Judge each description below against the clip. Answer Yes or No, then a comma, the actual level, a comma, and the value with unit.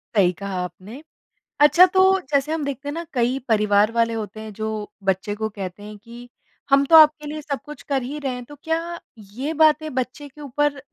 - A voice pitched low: No, very high, 265 Hz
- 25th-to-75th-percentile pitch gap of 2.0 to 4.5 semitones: No, wide, 5.6 semitones